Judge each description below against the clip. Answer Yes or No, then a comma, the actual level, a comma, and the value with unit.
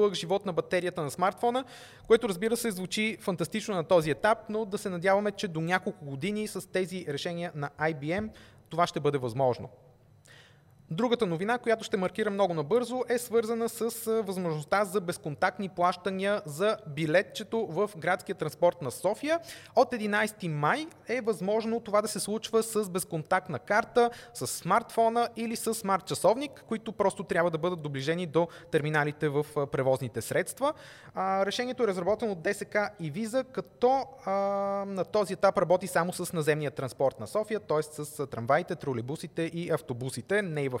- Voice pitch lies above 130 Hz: Yes, high, 190 Hz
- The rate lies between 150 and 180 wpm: Yes, average, 155 wpm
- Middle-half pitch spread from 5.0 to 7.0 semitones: Yes, wide, 5.4 semitones